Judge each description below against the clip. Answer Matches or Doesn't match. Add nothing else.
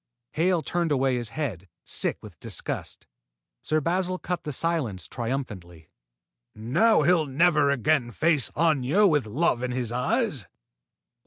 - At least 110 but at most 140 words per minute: Matches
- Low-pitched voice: Doesn't match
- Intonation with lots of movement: Matches